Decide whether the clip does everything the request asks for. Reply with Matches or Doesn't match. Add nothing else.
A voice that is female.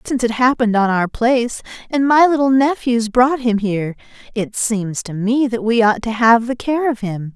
Matches